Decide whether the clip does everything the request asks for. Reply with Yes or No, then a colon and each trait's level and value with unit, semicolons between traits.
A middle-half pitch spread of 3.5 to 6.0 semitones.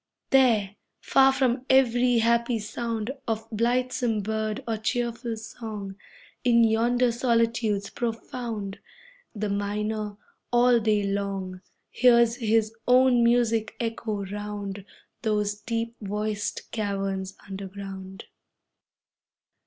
No: narrow, 2.5 semitones